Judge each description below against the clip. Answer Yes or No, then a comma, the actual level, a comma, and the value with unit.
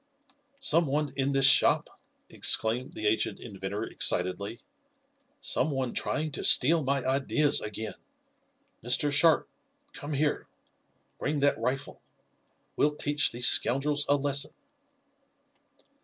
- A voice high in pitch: No, low, 135 Hz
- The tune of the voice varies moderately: Yes, average, 3.4 semitones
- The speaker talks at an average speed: No, slow, 115 wpm